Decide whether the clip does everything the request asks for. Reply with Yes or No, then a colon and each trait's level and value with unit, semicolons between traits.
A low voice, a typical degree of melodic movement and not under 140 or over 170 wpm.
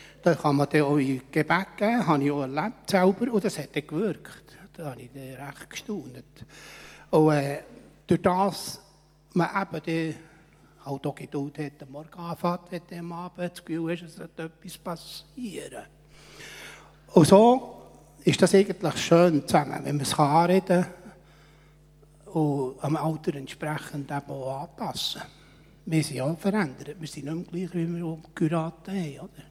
No: medium, 160 Hz; average, 3.2 semitones; average, 165 wpm